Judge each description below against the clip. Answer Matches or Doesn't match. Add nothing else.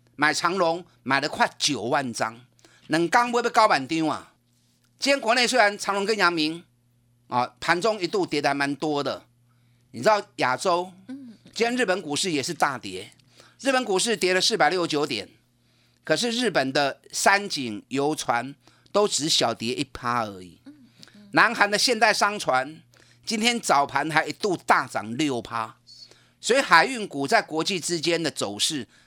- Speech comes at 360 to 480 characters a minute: Doesn't match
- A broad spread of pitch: Matches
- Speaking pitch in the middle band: Matches